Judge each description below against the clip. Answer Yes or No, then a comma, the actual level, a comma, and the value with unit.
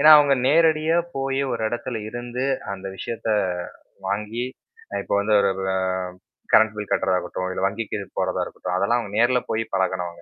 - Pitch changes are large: No, average, 4.2 semitones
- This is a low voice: Yes, low, 110 Hz